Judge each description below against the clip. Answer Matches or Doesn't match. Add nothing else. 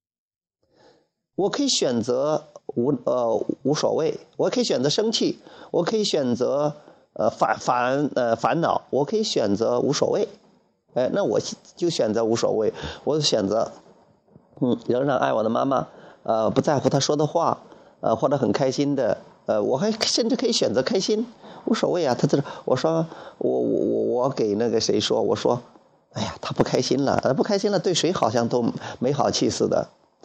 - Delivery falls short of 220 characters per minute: Doesn't match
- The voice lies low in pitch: Doesn't match